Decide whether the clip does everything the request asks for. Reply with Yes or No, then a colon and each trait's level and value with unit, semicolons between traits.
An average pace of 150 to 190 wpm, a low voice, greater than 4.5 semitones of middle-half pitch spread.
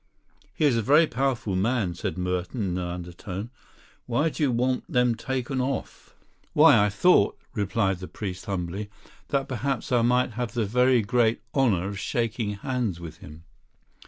Yes: average, 165 wpm; low, 115 Hz; average, 4.9 semitones